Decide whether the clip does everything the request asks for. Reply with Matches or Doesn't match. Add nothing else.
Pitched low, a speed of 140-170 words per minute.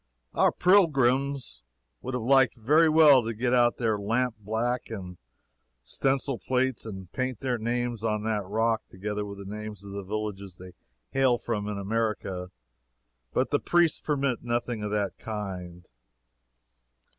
Matches